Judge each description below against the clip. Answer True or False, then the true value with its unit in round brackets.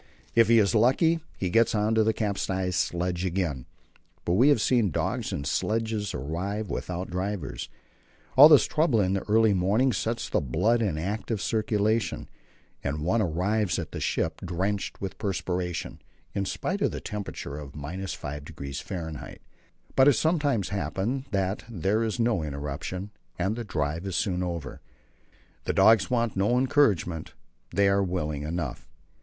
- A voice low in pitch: True (100 Hz)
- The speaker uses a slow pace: False (155 wpm)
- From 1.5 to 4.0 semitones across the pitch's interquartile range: False (4.4 semitones)